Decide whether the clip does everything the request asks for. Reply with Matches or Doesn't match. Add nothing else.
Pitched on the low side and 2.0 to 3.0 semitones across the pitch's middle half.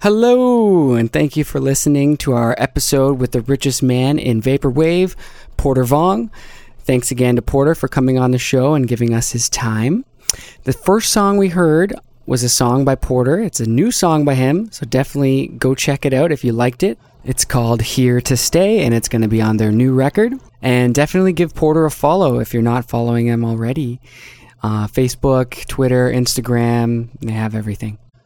Doesn't match